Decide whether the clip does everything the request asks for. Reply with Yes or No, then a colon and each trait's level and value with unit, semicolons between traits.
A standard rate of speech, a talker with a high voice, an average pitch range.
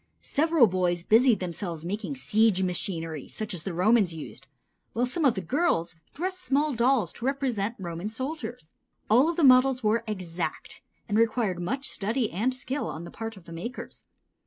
No: average, 175 wpm; high, 220 Hz; wide, 6.4 semitones